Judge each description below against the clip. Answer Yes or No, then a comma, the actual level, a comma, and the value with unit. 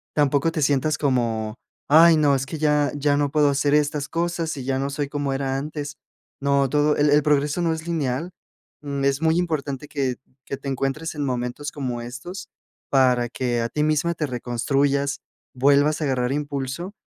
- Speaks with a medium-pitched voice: Yes, medium, 145 Hz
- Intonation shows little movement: Yes, narrow, 2.1 semitones